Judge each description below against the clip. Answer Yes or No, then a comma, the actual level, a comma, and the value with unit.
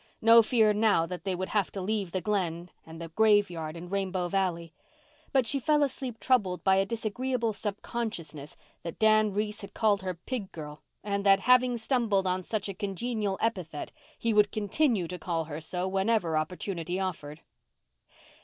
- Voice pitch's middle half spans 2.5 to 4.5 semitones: Yes, average, 3.8 semitones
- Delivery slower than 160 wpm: No, average, 170 wpm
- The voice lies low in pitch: No, high, 195 Hz